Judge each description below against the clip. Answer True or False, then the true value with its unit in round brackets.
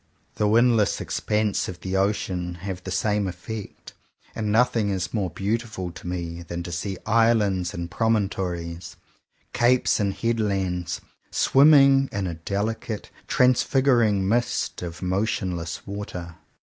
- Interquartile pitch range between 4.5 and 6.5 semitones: False (4.0 semitones)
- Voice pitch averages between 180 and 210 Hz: False (100 Hz)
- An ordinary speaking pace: False (130 wpm)